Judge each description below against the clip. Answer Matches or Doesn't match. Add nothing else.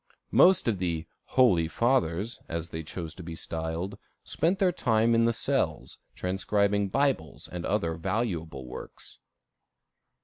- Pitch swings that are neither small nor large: Doesn't match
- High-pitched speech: Doesn't match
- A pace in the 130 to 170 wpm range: Matches